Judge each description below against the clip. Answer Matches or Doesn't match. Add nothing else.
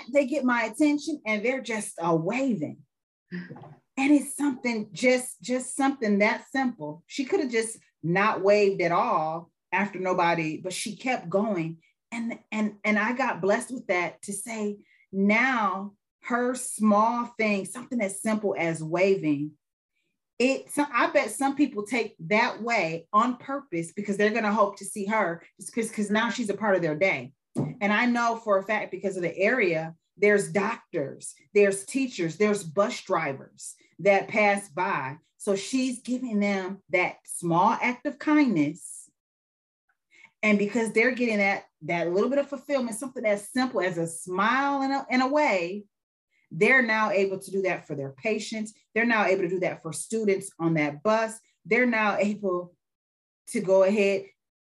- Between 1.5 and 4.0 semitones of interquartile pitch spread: Doesn't match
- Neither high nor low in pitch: Doesn't match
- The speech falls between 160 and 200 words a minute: Matches